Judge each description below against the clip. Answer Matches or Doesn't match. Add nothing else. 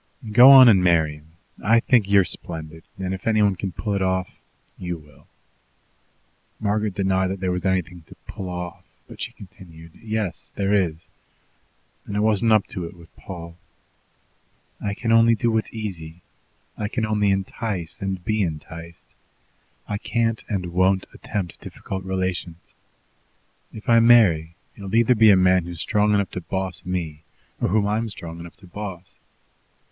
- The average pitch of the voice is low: Matches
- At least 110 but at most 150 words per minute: Doesn't match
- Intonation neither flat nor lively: Matches